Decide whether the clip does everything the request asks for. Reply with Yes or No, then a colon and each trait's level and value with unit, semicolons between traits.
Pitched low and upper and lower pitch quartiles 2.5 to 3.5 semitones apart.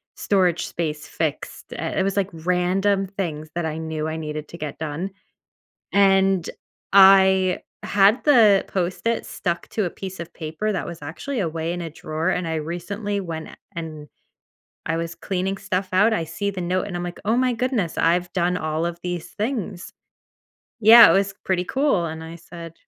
No: medium, 180 Hz; average, 3.2 semitones